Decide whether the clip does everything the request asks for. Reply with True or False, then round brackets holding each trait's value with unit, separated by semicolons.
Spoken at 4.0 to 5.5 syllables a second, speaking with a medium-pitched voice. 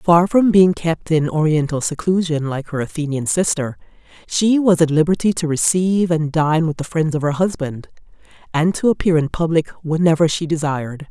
True (5.1 syllables/s; 160 Hz)